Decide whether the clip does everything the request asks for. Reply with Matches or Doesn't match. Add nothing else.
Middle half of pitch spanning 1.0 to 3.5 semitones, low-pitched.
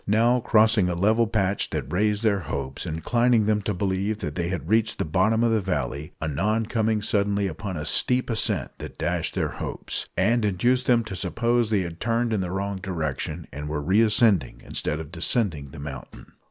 Doesn't match